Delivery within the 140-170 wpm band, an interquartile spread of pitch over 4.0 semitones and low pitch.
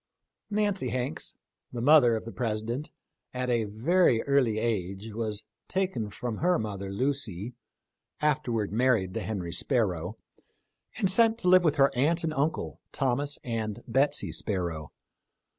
Yes: average, 150 wpm; wide, 5.5 semitones; low, 120 Hz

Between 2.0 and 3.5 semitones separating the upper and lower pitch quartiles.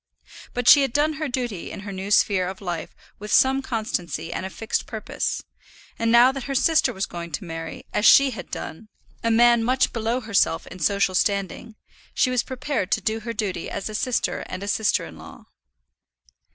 No: average, 4.7 semitones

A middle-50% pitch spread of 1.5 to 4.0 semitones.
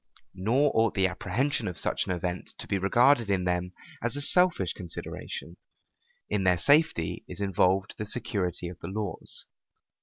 No: average, 4.6 semitones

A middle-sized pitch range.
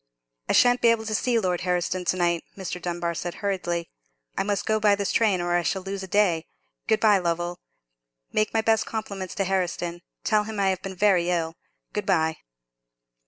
Yes: average, 3.1 semitones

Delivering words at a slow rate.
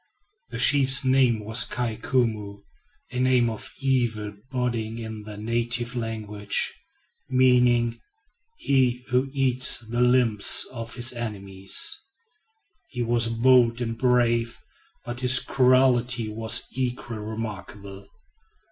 Yes: slow, 110 wpm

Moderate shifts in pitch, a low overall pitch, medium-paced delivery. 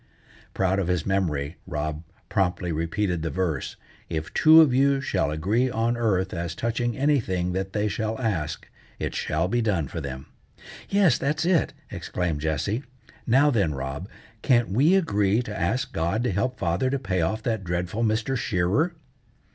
No: wide, 6.1 semitones; low, 100 Hz; average, 165 wpm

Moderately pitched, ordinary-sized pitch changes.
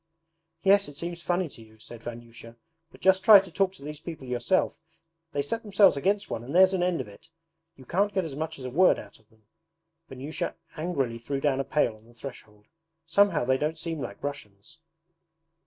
No: medium, 145 Hz; wide, 7.0 semitones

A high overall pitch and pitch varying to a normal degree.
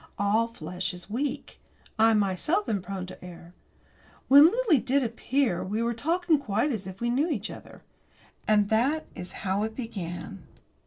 No: high, 220 Hz; wide, 6.3 semitones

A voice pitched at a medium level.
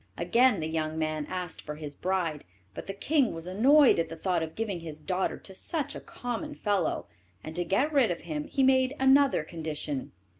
Yes: medium, 180 Hz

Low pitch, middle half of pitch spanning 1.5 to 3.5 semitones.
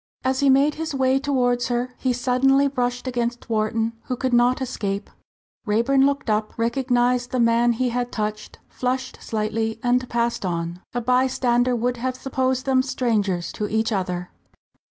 No: high, 245 Hz; narrow, 2.5 semitones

